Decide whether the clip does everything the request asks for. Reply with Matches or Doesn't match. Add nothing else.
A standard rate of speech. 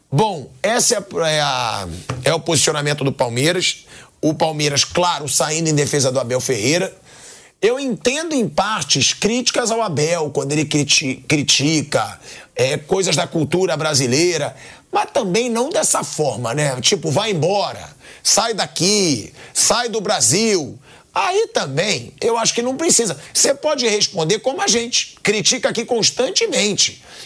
Matches